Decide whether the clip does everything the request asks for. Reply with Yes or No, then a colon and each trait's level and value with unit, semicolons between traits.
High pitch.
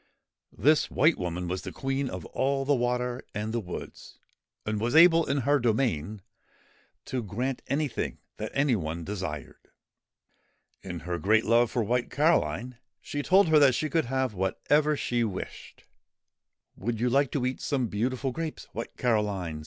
No: low, 120 Hz